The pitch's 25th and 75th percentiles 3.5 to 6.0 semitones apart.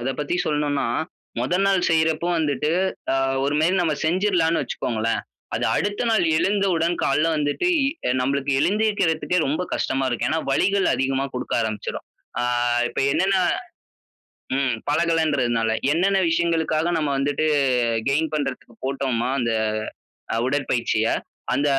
Yes: average, 4.0 semitones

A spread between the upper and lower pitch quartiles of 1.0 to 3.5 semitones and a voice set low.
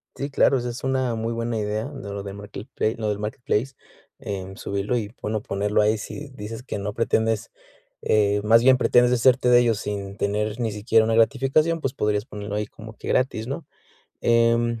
Yes: average, 2.8 semitones; low, 110 Hz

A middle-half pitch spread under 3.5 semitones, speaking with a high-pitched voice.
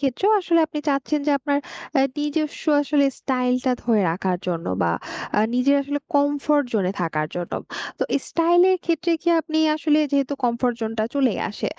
No: average, 4.2 semitones; very high, 280 Hz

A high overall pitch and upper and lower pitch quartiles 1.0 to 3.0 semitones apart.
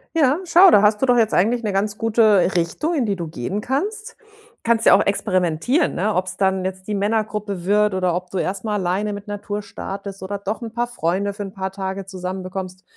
Yes: high, 200 Hz; average, 2.7 semitones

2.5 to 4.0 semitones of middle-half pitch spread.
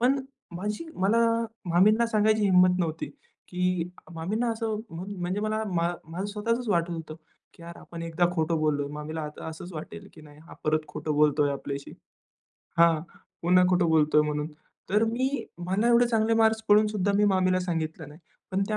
No: average, 4.8 semitones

